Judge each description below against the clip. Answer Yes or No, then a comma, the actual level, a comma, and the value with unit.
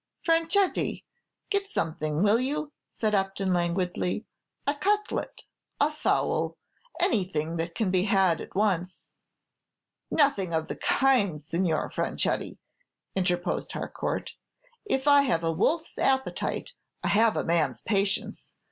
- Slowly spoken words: Yes, slow, 120 wpm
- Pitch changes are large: Yes, wide, 8.2 semitones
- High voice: Yes, high, 195 Hz